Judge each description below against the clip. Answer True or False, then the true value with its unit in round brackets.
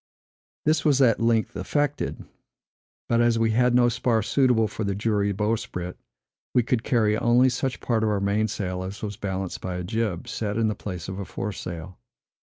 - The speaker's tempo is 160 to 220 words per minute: True (180 wpm)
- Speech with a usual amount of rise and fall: True (3.1 semitones)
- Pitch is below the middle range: True (110 Hz)